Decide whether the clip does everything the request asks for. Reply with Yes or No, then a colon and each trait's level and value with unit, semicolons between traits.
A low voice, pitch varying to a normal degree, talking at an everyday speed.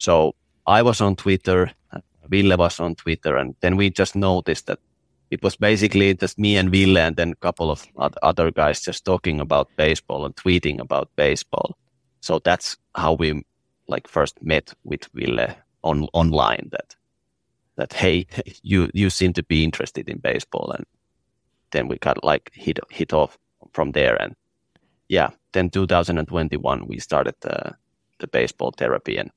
Yes: very low, 90 Hz; average, 3.0 semitones; average, 165 wpm